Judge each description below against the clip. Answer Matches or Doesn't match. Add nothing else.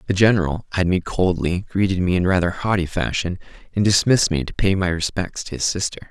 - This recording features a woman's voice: Doesn't match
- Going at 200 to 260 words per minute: Matches